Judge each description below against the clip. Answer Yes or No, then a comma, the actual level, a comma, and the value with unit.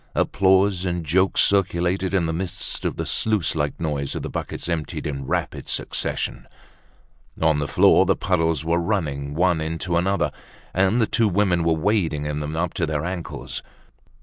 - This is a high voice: No, very low, 85 Hz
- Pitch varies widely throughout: No, average, 3.3 semitones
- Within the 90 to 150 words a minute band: No, average, 175 wpm